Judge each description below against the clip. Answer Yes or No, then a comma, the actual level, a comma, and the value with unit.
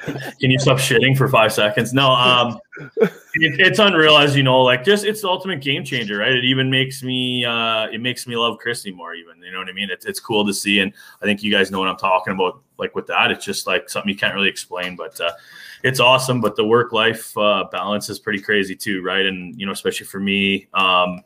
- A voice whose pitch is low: Yes, low, 115 Hz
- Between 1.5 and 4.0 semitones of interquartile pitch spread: No, average, 5.1 semitones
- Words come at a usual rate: No, fast, 245 wpm